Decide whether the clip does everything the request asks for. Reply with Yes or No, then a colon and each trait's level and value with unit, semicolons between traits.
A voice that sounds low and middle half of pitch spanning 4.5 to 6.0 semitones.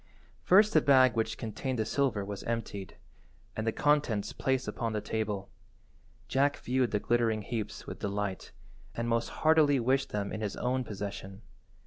No: low, 115 Hz; average, 4.1 semitones